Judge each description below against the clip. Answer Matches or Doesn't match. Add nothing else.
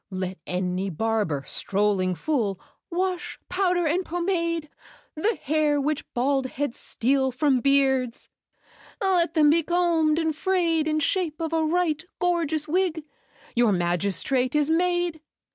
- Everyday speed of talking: Doesn't match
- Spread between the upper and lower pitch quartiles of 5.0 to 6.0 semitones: Matches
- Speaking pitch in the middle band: Doesn't match